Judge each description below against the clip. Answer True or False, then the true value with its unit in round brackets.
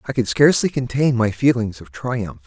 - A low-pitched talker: True (115 Hz)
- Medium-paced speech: True (195 wpm)